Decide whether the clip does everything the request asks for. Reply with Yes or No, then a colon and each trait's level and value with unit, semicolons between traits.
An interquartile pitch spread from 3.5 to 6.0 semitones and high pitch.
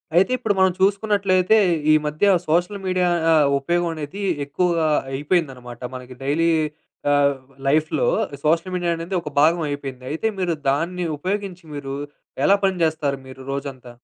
No: average, 4.4 semitones; medium, 165 Hz